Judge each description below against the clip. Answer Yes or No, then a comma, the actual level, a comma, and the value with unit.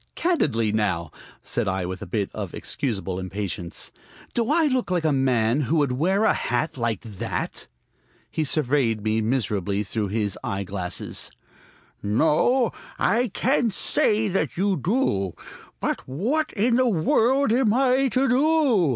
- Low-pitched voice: No, medium, 145 Hz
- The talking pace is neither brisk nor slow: Yes, average, 150 wpm